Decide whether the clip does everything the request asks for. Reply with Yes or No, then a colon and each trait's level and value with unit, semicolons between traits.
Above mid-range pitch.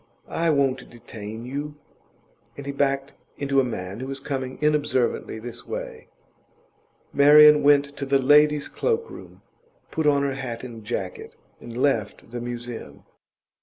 No: low, 135 Hz